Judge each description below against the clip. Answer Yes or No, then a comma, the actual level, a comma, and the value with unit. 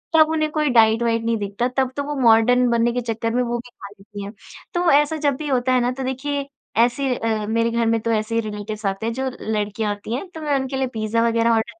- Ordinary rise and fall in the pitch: Yes, average, 3.1 semitones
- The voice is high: Yes, high, 235 Hz